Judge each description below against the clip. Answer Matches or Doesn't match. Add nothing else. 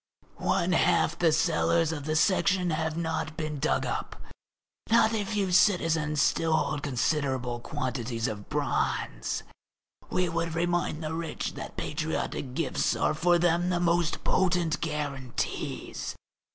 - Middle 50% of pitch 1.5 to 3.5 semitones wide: Matches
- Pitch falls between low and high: Matches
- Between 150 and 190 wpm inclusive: Doesn't match